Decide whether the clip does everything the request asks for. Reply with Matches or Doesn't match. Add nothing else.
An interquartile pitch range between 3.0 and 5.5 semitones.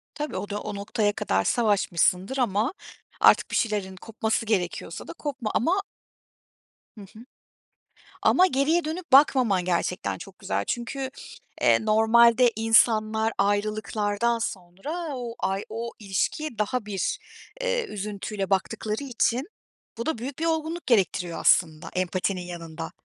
Matches